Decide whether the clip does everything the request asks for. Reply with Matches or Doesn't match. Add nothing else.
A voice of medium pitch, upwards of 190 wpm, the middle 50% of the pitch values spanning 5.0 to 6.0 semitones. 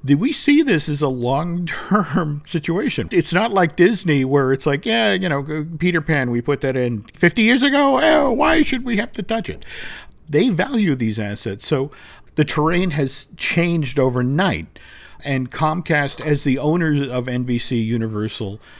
Doesn't match